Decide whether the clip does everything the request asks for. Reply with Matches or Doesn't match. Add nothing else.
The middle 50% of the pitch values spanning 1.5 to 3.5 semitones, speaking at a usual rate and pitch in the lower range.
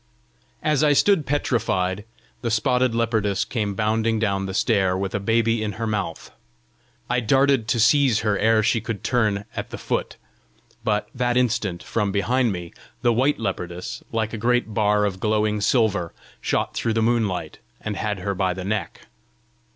Matches